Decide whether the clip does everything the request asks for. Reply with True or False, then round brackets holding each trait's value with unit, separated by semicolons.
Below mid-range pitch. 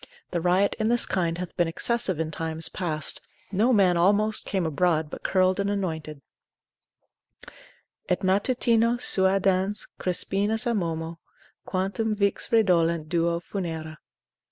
False (185 Hz)